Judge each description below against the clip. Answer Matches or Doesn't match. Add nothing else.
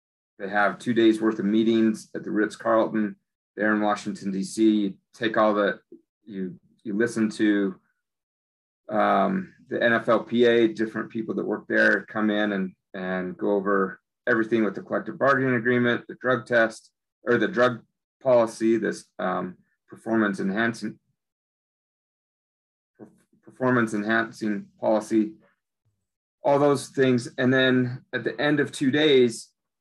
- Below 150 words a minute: Matches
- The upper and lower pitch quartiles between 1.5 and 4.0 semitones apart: Matches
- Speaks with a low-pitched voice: Matches